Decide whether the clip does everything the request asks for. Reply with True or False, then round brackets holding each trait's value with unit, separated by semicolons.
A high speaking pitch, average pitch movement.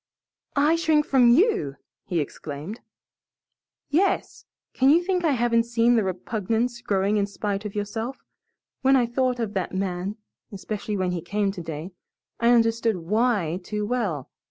True (220 Hz; 4.3 semitones)